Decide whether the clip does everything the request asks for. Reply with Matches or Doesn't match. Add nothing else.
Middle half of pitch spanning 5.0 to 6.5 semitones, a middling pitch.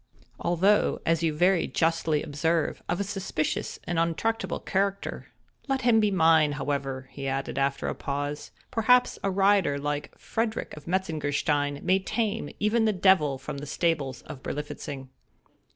Matches